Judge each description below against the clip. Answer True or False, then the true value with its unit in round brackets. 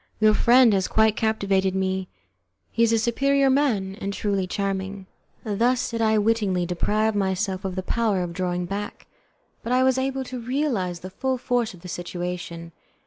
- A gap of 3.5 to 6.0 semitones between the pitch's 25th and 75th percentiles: True (3.8 semitones)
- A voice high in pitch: True (205 Hz)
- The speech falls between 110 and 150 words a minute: False (175 wpm)